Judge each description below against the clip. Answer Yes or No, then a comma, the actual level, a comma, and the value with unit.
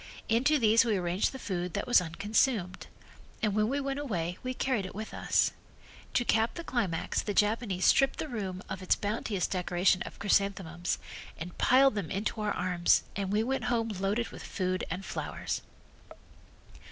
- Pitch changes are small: No, average, 4.3 semitones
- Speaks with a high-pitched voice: Yes, high, 205 Hz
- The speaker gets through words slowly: No, average, 175 wpm